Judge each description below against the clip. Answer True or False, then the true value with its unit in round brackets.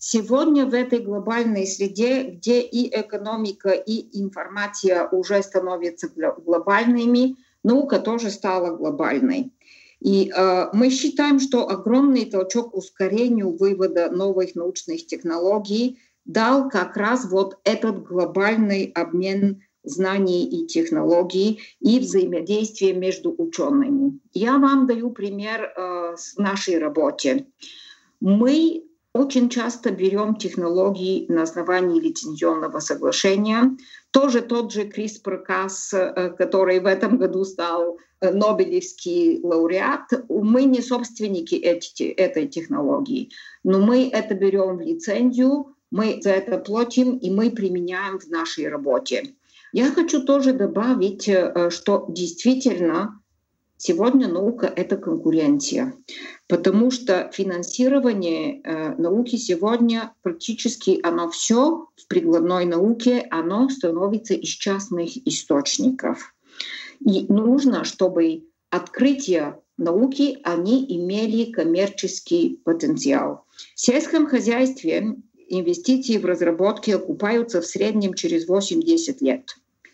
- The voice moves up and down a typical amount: False (5.7 semitones)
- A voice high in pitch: True (210 Hz)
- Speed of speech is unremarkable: False (105 wpm)